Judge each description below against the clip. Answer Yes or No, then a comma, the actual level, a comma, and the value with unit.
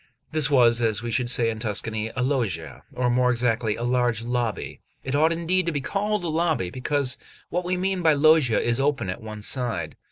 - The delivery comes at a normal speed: No, fast, 210 wpm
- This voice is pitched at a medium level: No, low, 125 Hz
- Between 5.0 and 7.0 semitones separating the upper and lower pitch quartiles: Yes, wide, 5.4 semitones